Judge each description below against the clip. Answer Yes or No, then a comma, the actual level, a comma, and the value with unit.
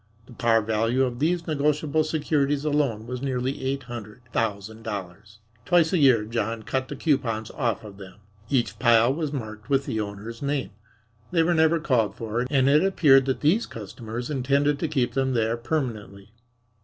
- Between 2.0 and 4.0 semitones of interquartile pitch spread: No, average, 4.6 semitones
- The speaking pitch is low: Yes, low, 125 Hz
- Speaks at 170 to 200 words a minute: Yes, average, 175 wpm